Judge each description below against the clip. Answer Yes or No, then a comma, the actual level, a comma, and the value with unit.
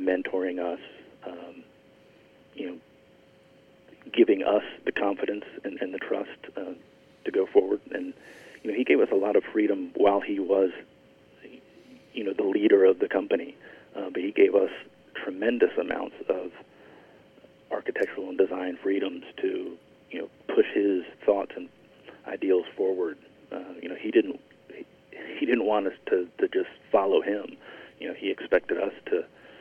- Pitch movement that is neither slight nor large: No, wide, 7.6 semitones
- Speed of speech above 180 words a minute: No, average, 160 wpm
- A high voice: Yes, very high, 385 Hz